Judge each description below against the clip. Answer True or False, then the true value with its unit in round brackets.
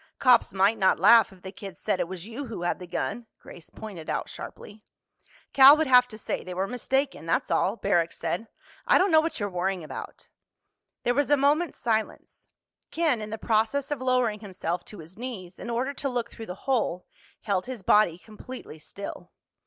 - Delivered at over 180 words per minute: True (200 wpm)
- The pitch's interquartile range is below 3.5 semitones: False (5.2 semitones)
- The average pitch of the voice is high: True (220 Hz)